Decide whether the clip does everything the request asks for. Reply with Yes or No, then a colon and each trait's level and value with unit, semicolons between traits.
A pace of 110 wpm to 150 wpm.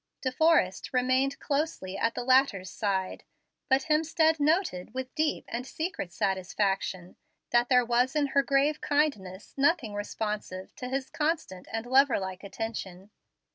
Yes: average, 140 wpm